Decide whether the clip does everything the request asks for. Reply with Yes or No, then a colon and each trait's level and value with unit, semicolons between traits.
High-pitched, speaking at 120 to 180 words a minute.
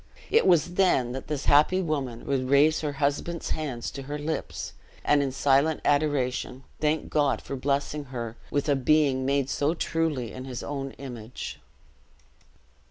No: medium, 140 Hz; average, 160 wpm